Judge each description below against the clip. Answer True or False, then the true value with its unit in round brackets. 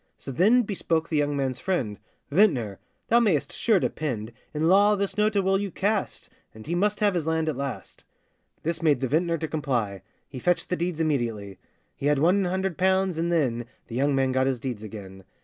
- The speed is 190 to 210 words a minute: True (205 wpm)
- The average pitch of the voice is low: False (160 Hz)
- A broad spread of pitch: True (6.4 semitones)